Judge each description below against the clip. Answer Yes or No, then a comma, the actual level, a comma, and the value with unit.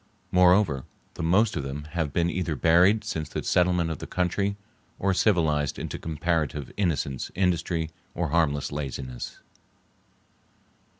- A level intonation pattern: No, average, 3.5 semitones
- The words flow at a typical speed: No, slow, 130 wpm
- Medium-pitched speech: No, very low, 85 Hz